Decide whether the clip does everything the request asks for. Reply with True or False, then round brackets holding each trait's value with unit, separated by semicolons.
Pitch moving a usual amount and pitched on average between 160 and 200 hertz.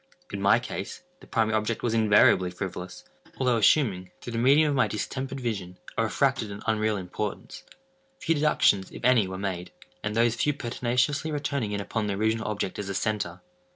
False (4.0 semitones; 110 Hz)